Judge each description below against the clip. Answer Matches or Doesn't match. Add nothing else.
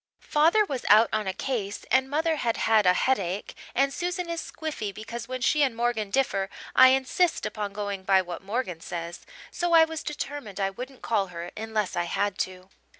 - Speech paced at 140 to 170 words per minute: Doesn't match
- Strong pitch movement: Matches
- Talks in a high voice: Matches